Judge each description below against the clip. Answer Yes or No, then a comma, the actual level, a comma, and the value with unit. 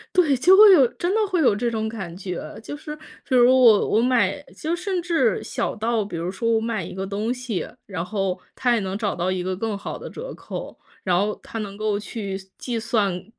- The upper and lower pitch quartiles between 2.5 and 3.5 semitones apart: No, average, 4.7 semitones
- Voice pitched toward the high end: Yes, high, 220 Hz